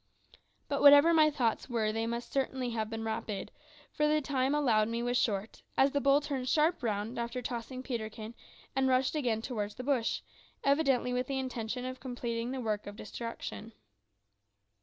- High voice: Yes, very high, 250 Hz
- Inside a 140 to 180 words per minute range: Yes, average, 170 wpm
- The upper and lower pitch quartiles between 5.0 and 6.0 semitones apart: No, average, 3.2 semitones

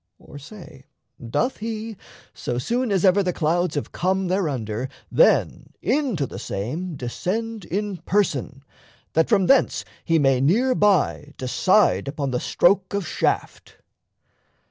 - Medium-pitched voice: Yes, medium, 180 Hz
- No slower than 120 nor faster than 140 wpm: Yes, slow, 135 wpm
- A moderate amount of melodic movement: No, wide, 6.8 semitones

